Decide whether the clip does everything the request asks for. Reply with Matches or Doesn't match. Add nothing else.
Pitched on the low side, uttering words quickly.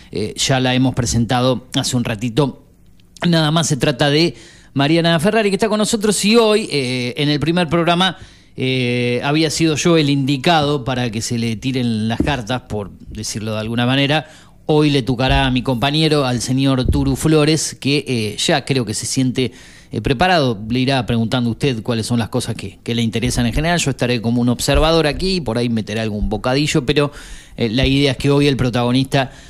Matches